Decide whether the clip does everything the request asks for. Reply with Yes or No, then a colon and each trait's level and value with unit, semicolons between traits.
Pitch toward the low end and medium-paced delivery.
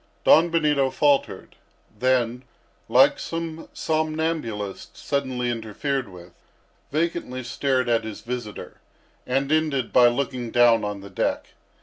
No: low, 130 Hz; slow, 115 wpm